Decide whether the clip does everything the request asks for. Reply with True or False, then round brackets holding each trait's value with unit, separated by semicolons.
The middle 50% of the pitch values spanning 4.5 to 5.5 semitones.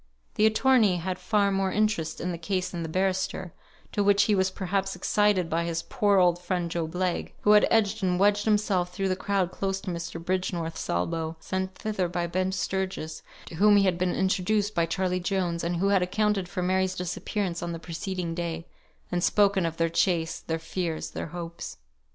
False (2.6 semitones)